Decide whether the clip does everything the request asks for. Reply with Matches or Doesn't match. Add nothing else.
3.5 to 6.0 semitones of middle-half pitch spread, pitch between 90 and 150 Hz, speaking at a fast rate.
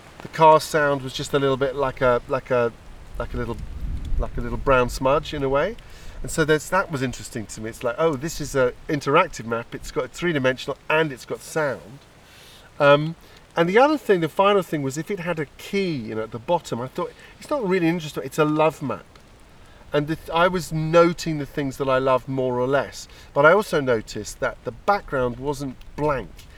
Matches